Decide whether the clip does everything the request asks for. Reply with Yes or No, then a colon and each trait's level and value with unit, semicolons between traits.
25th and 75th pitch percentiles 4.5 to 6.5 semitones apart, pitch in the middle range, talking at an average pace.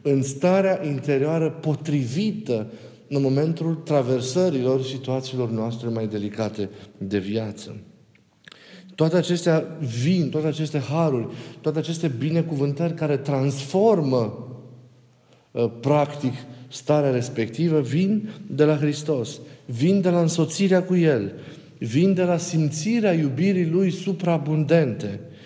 No: average, 4.8 semitones; medium, 150 Hz; slow, 105 wpm